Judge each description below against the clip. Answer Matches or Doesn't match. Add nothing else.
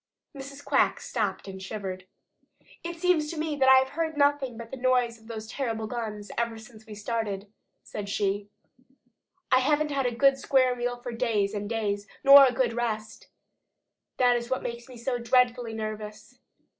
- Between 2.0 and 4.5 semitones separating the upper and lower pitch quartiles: Matches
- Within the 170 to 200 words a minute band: Matches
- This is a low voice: Doesn't match